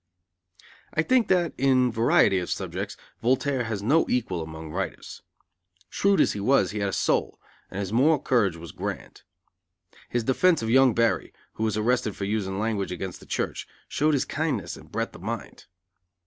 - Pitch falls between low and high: No, low, 115 Hz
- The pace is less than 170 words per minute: No, average, 175 wpm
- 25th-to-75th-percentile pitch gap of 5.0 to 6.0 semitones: Yes, wide, 5.4 semitones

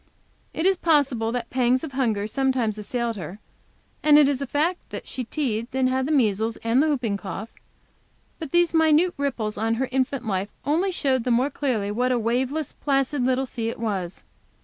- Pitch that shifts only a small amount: No, average, 4.0 semitones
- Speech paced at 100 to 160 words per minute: No, average, 190 wpm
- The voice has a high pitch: Yes, very high, 255 Hz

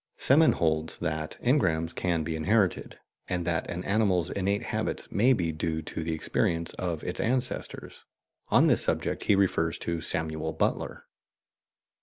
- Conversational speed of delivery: Yes, average, 150 wpm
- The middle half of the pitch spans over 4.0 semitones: No, average, 3.7 semitones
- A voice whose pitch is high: No, very low, 85 Hz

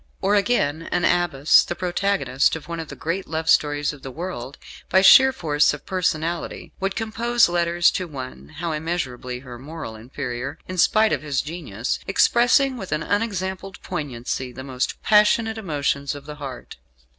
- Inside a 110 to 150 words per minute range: No, average, 170 wpm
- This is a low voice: No, medium, 160 Hz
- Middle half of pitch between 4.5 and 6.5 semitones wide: Yes, average, 5.2 semitones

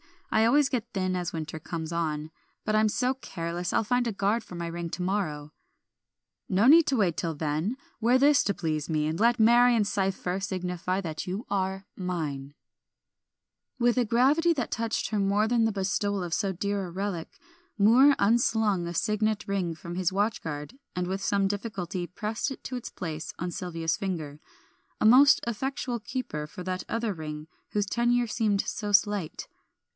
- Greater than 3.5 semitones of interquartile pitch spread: Yes, average, 4.9 semitones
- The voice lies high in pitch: Yes, high, 200 Hz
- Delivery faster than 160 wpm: Yes, average, 180 wpm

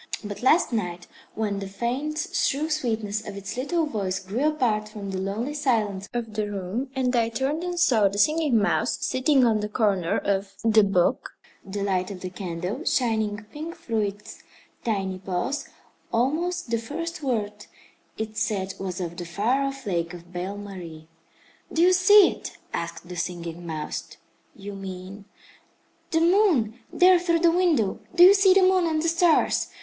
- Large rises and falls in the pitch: Yes, wide, 7.3 semitones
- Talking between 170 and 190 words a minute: Yes, average, 175 wpm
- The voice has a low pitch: No, high, 220 Hz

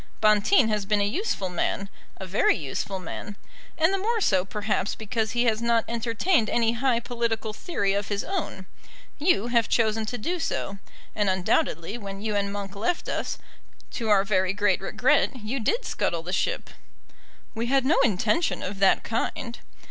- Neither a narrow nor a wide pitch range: Yes, average, 3.3 semitones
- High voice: Yes, high, 220 Hz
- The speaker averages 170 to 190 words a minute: Yes, average, 175 wpm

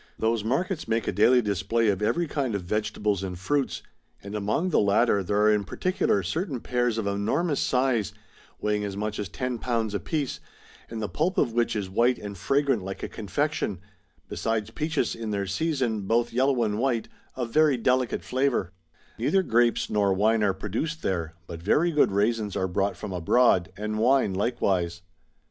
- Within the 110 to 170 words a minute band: No, average, 180 wpm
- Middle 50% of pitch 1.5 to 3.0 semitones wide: No, average, 4.1 semitones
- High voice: No, low, 110 Hz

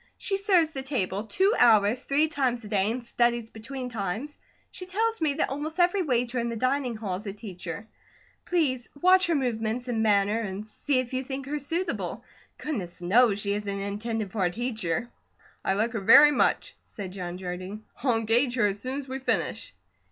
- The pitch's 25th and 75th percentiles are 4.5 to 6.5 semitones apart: Yes, average, 5.2 semitones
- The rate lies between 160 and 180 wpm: No, average, 195 wpm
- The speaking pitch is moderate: No, high, 235 Hz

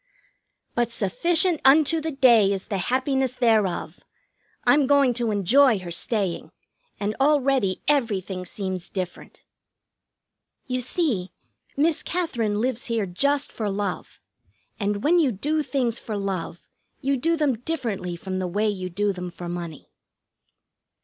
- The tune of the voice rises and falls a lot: Yes, wide, 6.3 semitones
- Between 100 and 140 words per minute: Yes, slow, 135 wpm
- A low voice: No, high, 225 Hz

